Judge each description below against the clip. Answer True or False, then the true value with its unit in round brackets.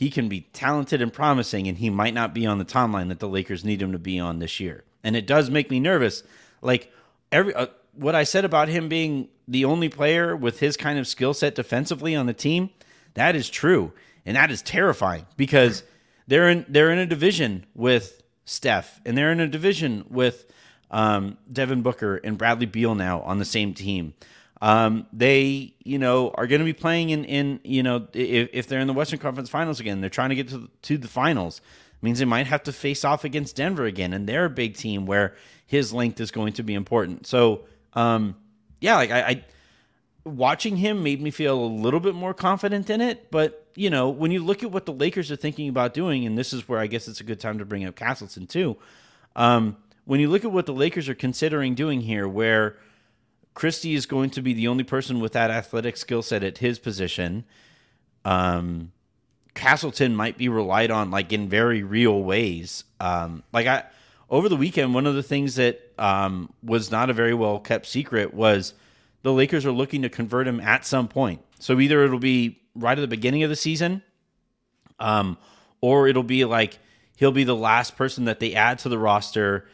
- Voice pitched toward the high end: False (125 Hz)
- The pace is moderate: False (215 wpm)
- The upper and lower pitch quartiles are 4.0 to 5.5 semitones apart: True (4.8 semitones)